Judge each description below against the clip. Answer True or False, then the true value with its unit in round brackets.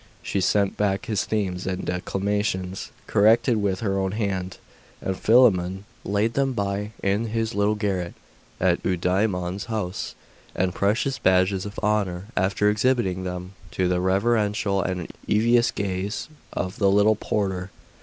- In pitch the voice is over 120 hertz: False (100 Hz)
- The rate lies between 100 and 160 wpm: True (140 wpm)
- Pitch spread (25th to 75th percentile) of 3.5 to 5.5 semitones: False (2.4 semitones)